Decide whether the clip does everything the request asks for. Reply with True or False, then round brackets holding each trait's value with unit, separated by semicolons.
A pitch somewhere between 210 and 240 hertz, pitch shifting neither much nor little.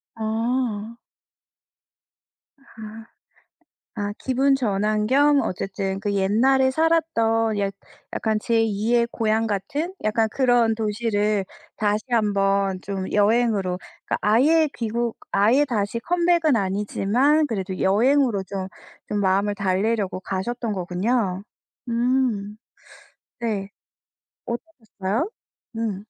True (220 Hz; 3.4 semitones)